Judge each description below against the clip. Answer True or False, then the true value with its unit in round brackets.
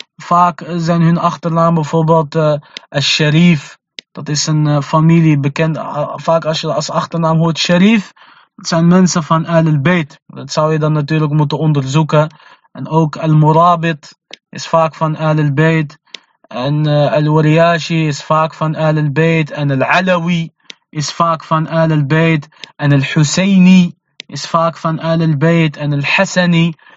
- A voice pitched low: False (160 Hz)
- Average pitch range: False (1.6 semitones)